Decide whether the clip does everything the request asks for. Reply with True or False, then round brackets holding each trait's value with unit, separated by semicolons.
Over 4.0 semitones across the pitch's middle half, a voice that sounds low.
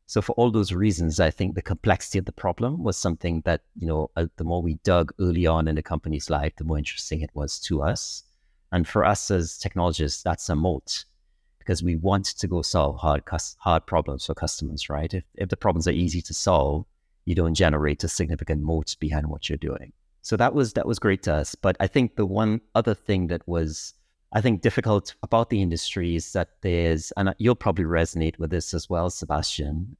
False (3.5 semitones; 85 Hz)